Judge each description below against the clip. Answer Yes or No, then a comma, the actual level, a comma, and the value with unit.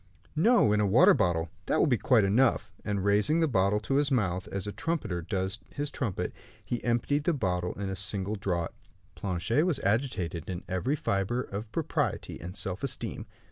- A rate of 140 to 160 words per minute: No, average, 185 wpm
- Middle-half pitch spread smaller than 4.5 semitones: No, wide, 5.6 semitones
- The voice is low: Yes, low, 105 Hz